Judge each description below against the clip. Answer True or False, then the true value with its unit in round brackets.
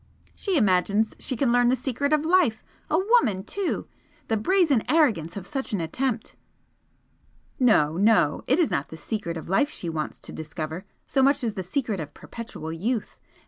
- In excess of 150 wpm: True (180 wpm)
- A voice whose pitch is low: False (225 Hz)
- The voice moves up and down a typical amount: False (7.8 semitones)